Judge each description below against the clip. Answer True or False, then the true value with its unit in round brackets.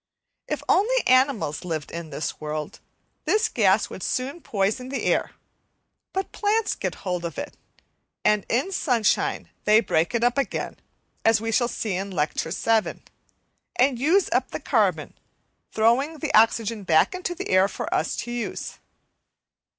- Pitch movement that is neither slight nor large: False (6.6 semitones)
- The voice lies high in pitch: True (230 Hz)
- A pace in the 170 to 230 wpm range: False (160 wpm)